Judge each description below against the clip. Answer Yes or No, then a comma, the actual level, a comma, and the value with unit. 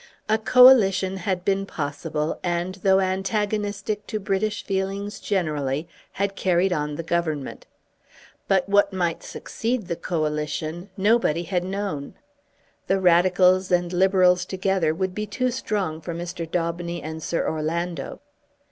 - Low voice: No, medium, 185 Hz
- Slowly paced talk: Yes, slow, 130 wpm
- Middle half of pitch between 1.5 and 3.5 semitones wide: Yes, average, 2.8 semitones